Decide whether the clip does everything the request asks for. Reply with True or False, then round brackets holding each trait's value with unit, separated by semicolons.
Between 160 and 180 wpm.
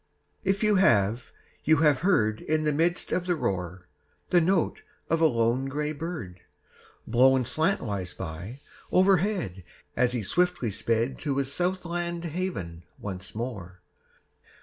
False (140 wpm)